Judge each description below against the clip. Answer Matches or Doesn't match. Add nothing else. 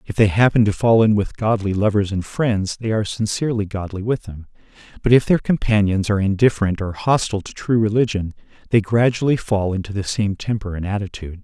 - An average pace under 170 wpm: Doesn't match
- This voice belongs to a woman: Doesn't match